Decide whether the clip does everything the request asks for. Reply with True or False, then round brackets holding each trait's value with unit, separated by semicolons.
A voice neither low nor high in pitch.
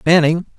True (165 Hz)